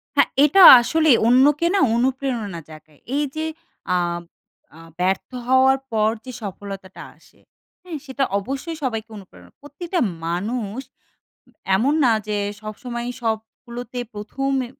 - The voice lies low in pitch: No, high, 240 Hz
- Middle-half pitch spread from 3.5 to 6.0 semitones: Yes, average, 4.8 semitones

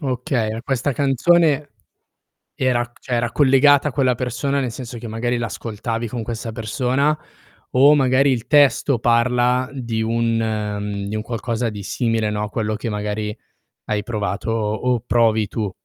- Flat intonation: No, average, 3.0 semitones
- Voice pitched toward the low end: Yes, low, 120 Hz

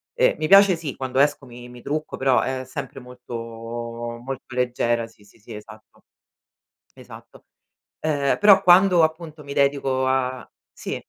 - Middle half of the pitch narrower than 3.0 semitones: No, average, 4.2 semitones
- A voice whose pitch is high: No, low, 130 Hz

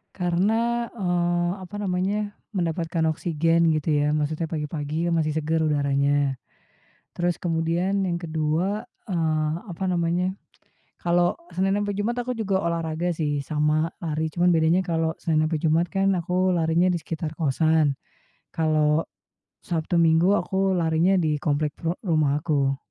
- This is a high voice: No, medium, 165 Hz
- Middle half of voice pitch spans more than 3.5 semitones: No, narrow, 2.6 semitones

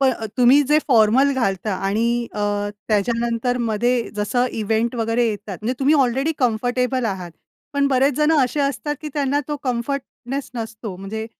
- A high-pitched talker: Yes, high, 245 Hz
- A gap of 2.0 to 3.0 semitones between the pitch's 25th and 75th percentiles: No, average, 3.7 semitones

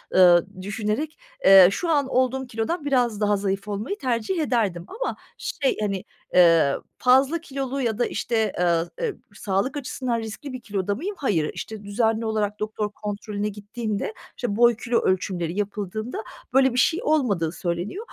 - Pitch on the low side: No, high, 220 Hz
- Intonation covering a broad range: No, average, 4.5 semitones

